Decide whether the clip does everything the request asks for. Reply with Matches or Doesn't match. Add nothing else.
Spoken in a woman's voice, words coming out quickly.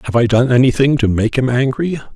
Doesn't match